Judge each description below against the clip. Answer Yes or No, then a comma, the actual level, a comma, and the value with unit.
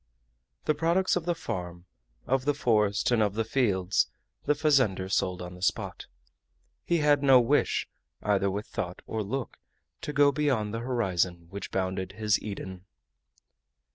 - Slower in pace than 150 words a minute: No, average, 155 wpm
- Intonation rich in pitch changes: Yes, wide, 6.5 semitones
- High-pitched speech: No, low, 110 Hz